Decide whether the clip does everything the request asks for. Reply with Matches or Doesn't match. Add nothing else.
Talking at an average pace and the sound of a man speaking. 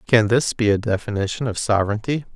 Matches